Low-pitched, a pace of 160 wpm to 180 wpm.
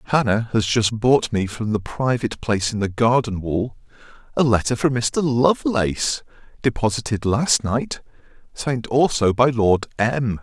No: low, 115 Hz; average, 150 wpm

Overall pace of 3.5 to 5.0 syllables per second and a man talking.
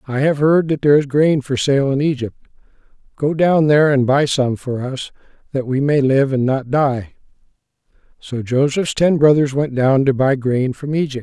Yes: 4.8 syllables/s; male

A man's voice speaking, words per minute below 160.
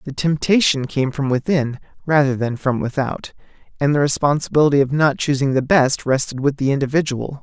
No: male; average, 170 wpm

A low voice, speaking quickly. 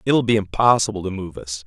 Yes: low, 100 Hz; fast, 215 wpm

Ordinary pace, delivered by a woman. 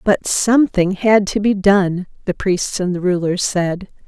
Yes: average, 175 wpm; female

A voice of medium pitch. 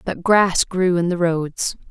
Yes: medium, 175 Hz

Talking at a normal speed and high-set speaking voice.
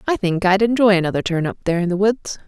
No: fast, 265 wpm; high, 195 Hz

